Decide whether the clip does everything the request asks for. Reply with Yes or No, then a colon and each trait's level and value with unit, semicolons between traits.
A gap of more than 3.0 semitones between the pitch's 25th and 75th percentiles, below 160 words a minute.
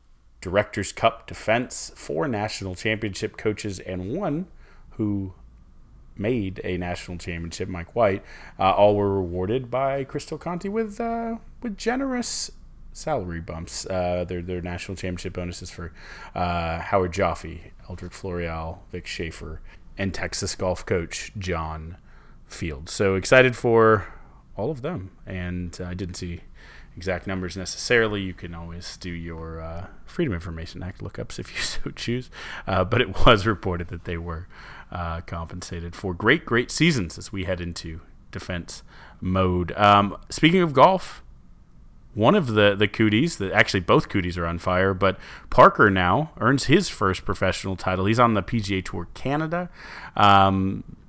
Yes: average, 3.8 semitones; average, 150 wpm